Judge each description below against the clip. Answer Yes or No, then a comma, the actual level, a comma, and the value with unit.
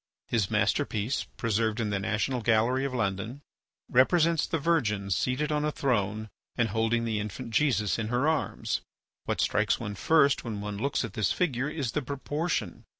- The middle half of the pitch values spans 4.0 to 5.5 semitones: Yes, average, 5.0 semitones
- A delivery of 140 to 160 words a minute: No, average, 170 wpm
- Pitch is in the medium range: No, low, 115 Hz